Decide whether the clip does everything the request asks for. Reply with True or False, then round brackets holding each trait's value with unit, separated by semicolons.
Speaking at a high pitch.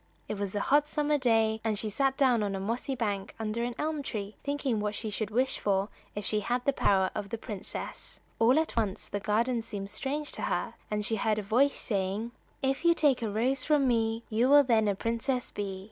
True (225 Hz)